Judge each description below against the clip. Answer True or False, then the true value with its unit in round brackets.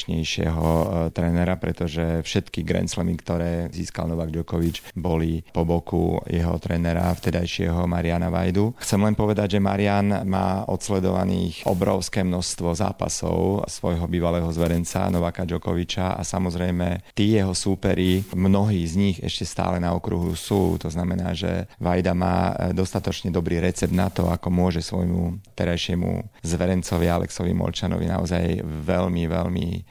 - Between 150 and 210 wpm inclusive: False (130 wpm)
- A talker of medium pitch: False (90 Hz)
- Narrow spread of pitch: True (2.0 semitones)